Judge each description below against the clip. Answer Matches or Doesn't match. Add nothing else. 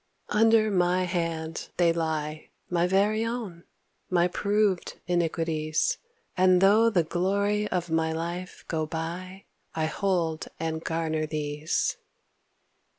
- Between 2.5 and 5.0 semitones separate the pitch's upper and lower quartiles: Matches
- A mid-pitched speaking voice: Matches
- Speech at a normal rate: Doesn't match